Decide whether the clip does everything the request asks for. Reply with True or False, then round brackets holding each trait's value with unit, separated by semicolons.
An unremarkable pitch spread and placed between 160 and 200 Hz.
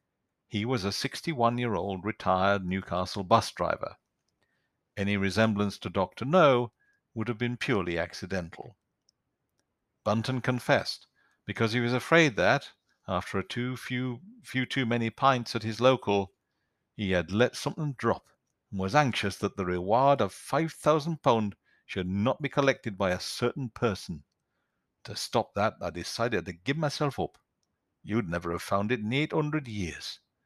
False (5.0 semitones; 115 Hz)